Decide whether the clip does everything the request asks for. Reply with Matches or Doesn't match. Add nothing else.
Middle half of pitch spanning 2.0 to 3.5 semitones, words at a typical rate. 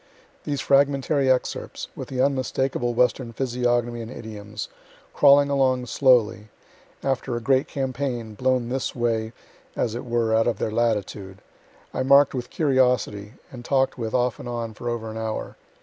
Matches